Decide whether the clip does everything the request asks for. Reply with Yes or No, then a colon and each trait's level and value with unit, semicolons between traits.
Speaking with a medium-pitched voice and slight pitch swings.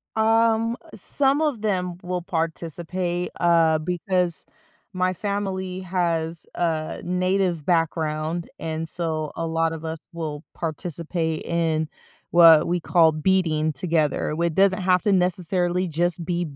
Yes: medium, 170 Hz; narrow, 2.3 semitones